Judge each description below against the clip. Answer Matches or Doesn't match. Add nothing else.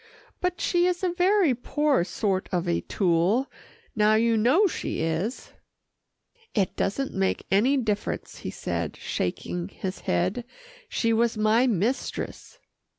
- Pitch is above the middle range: Matches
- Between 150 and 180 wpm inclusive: Doesn't match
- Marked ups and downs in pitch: Matches